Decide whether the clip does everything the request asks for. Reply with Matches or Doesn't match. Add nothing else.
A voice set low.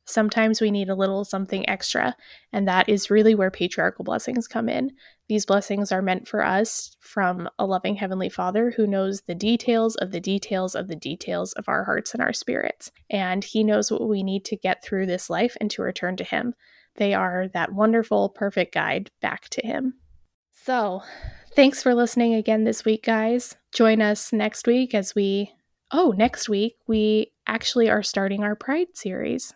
Doesn't match